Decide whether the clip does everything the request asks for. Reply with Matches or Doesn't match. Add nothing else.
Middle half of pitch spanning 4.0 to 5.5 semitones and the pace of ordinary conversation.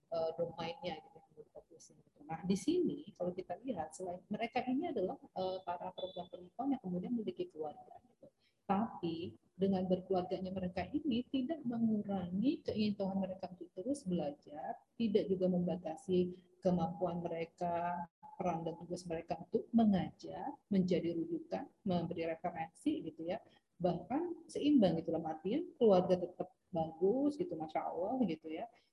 Doesn't match